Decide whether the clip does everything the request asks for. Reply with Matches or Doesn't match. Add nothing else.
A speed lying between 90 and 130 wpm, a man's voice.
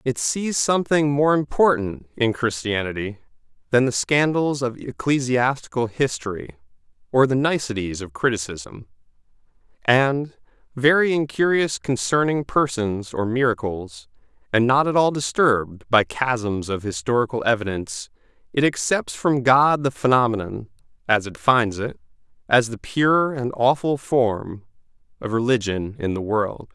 Matches